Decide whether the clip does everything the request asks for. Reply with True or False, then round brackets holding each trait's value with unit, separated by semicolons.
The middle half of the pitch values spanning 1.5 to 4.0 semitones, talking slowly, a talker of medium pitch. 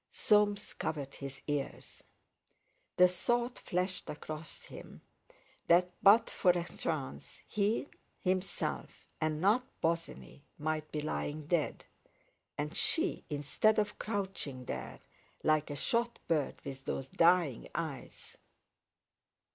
False (5.3 semitones; 115 wpm; 165 Hz)